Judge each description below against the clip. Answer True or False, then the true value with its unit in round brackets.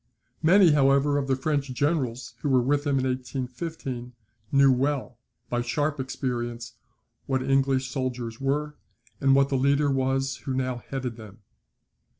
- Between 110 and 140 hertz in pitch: True (135 Hz)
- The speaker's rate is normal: True (150 wpm)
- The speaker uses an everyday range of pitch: False (1.9 semitones)